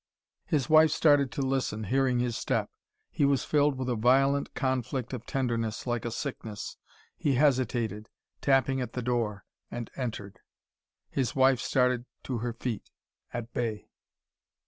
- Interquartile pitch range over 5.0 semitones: No, narrow, 2.5 semitones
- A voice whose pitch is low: Yes, low, 125 Hz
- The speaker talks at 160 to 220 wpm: No, average, 145 wpm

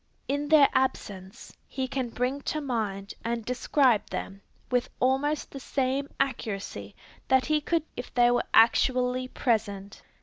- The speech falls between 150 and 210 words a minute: No, average, 140 wpm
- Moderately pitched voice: No, very high, 255 Hz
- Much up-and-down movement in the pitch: No, average, 3.4 semitones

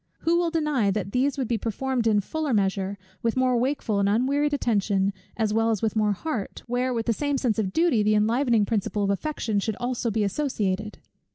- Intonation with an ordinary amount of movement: Yes, average, 4.2 semitones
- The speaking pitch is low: No, high, 225 Hz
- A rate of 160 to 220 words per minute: Yes, fast, 205 wpm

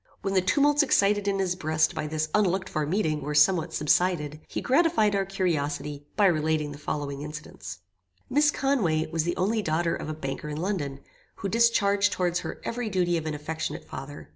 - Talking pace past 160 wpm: Yes, average, 190 wpm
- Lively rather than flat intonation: No, average, 4.8 semitones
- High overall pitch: No, medium, 170 Hz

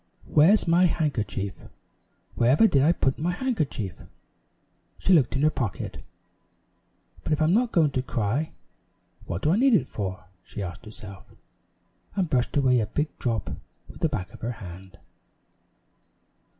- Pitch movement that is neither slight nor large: No, wide, 7.6 semitones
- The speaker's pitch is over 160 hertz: No, low, 135 Hz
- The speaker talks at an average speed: Yes, average, 155 wpm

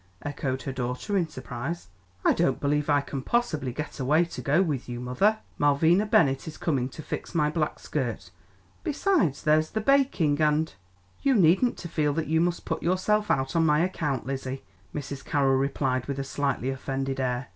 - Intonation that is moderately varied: Yes, average, 4.1 semitones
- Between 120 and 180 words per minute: No, average, 190 wpm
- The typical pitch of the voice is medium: Yes, medium, 150 Hz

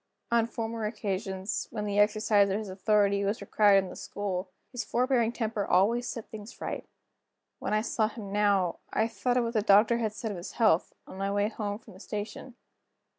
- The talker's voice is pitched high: Yes, high, 210 Hz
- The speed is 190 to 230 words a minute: Yes, average, 200 wpm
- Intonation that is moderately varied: No, narrow, 2.2 semitones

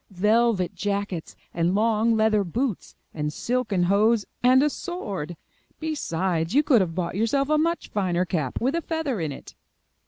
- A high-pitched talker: Yes, high, 210 Hz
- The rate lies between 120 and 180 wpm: Yes, average, 160 wpm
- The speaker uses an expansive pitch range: Yes, wide, 6.1 semitones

